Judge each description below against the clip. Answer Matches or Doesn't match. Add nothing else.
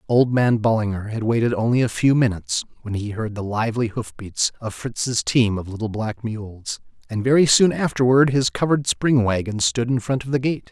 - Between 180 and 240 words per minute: Matches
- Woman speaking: Doesn't match